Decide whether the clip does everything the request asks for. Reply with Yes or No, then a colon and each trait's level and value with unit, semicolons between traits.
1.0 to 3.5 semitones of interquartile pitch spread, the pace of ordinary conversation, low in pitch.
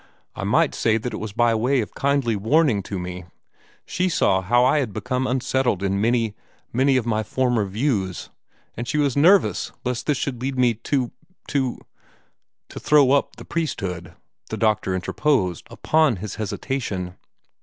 No: average, 5.0 semitones; average, 170 wpm; low, 120 Hz